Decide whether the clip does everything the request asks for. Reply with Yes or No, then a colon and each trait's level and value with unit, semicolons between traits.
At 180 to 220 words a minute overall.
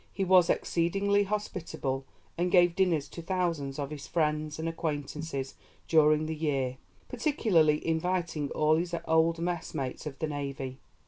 No: average, 140 wpm